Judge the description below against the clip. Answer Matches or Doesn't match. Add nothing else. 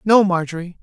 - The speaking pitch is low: Doesn't match